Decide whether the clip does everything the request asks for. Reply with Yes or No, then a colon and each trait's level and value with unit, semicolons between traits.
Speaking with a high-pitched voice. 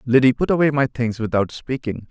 No: low, 125 Hz